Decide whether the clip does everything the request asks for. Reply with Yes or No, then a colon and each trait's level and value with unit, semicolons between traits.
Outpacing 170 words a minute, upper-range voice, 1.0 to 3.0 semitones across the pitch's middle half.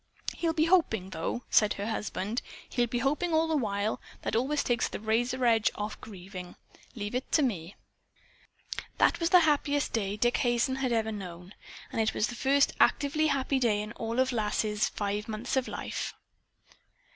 No: average, 180 wpm; high, 235 Hz; average, 4.4 semitones